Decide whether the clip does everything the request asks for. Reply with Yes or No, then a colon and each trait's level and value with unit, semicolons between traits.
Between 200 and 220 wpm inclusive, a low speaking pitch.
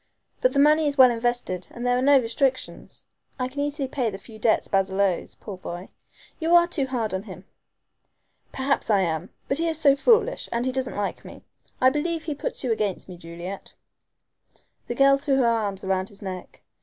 No: fast, 205 wpm; high, 245 Hz